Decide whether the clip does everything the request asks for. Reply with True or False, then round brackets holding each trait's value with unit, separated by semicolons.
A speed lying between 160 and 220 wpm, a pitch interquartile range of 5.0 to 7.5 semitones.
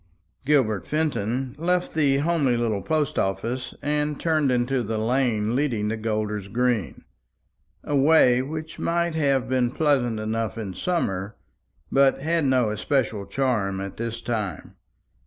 False (140 wpm; 5.3 semitones)